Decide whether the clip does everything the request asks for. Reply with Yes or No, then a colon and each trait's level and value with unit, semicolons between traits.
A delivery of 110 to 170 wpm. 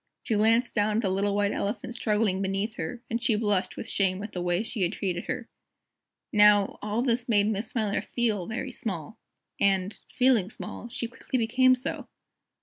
No: average, 185 wpm